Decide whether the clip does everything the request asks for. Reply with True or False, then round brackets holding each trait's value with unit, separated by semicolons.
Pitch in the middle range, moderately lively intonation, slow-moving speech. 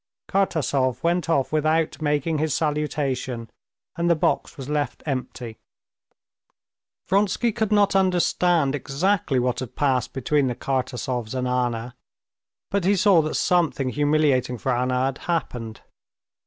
True (145 Hz; 4.9 semitones; 130 wpm)